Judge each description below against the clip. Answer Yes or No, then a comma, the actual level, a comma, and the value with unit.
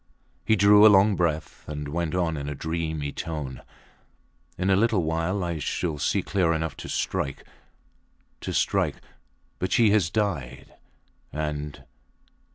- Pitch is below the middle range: Yes, very low, 80 Hz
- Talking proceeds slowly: No, average, 145 wpm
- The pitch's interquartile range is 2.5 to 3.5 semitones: No, average, 4.2 semitones